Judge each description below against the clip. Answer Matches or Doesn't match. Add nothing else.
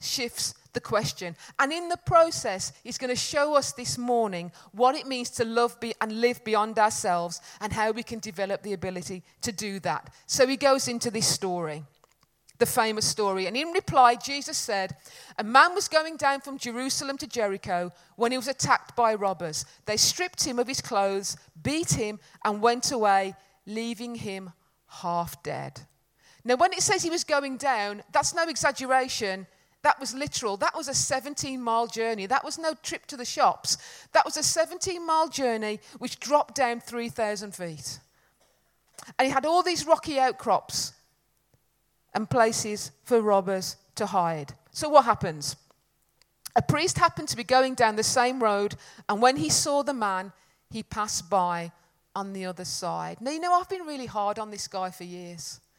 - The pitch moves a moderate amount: Doesn't match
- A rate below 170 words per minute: Doesn't match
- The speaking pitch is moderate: Doesn't match